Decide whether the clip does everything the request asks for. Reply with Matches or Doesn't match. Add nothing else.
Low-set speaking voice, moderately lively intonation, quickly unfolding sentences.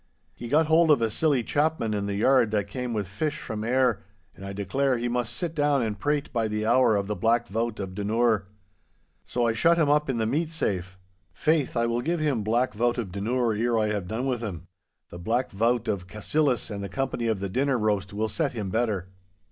Matches